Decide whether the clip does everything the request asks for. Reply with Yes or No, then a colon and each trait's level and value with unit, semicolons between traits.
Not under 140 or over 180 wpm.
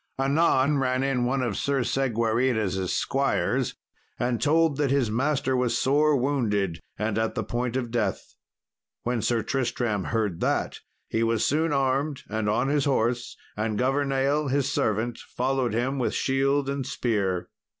Yes: average, 150 wpm